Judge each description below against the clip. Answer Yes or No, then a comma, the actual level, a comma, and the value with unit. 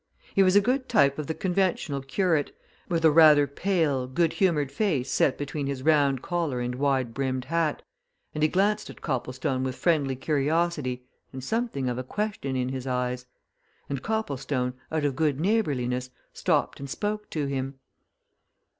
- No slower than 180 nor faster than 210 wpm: No, average, 165 wpm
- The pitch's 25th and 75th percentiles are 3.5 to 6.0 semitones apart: Yes, average, 4.6 semitones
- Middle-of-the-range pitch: Yes, medium, 145 Hz